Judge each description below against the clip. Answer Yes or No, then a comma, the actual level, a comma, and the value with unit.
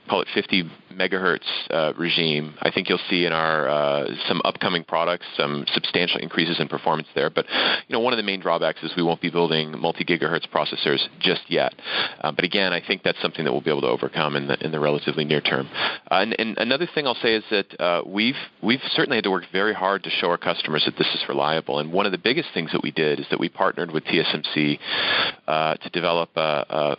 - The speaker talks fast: Yes, fast, 235 wpm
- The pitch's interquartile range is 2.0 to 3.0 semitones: Yes, narrow, 2.5 semitones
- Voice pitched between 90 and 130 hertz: No, very low, 80 Hz